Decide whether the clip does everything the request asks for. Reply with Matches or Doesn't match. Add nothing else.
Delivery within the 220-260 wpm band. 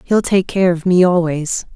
Doesn't match